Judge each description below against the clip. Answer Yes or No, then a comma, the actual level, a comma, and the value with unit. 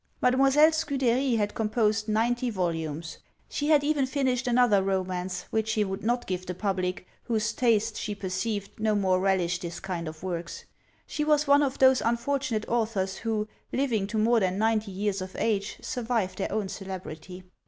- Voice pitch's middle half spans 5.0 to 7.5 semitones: No, average, 4.4 semitones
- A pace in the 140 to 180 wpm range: Yes, average, 170 wpm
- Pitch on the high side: Yes, high, 215 Hz